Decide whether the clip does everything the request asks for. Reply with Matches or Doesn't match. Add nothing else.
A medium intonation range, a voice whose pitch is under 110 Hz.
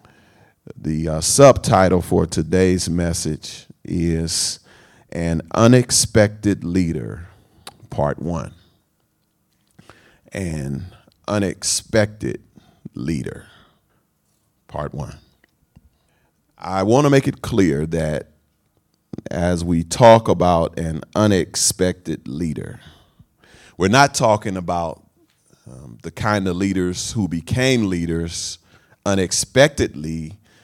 Matches